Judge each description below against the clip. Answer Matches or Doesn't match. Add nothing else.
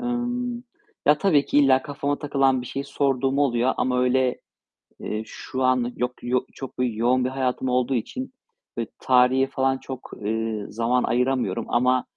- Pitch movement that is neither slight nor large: Doesn't match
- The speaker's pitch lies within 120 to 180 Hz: Matches